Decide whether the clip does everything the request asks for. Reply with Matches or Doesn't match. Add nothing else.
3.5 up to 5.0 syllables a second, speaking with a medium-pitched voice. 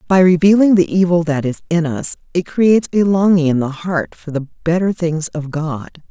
Matches